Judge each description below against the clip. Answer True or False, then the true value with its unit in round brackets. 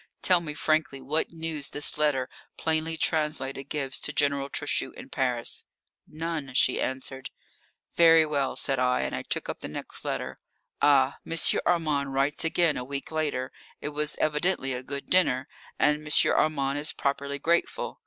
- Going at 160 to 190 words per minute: True (165 wpm)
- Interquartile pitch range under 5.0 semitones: True (2.7 semitones)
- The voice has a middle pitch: True (145 Hz)